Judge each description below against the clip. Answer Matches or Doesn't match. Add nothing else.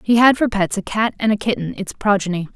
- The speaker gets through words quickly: Matches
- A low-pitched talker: Doesn't match